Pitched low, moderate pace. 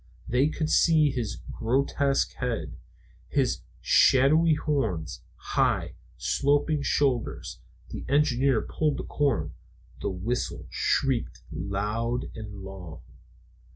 No: low, 130 Hz; slow, 100 wpm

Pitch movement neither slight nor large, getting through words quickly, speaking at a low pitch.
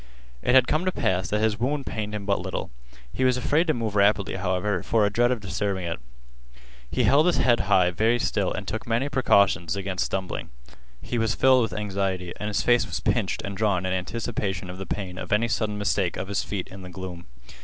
Yes: average, 3.9 semitones; fast, 220 wpm; low, 105 Hz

